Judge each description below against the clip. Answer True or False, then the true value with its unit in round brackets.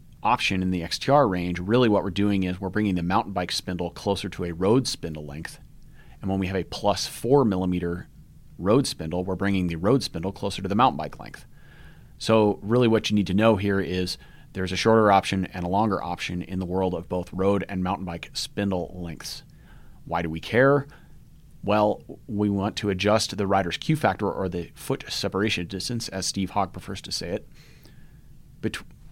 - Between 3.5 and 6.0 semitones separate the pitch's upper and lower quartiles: False (2.5 semitones)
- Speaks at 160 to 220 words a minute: True (200 wpm)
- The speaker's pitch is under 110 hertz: True (95 Hz)